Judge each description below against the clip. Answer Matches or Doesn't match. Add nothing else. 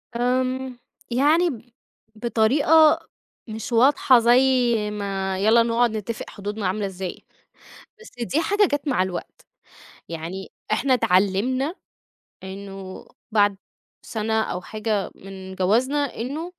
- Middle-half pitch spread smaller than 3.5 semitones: Doesn't match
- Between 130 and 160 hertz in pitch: Doesn't match